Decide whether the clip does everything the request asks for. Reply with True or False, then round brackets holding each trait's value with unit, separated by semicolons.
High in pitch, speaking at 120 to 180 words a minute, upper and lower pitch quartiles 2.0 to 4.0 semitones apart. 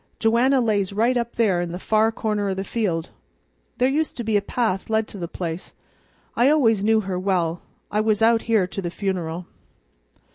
False (210 Hz; 195 wpm; 3.5 semitones)